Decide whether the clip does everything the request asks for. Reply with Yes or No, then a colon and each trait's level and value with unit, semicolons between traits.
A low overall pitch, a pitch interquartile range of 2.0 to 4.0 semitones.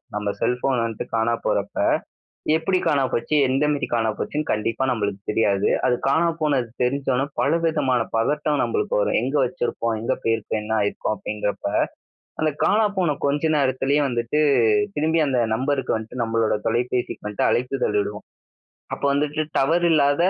No: low, 130 Hz; average, 4.7 semitones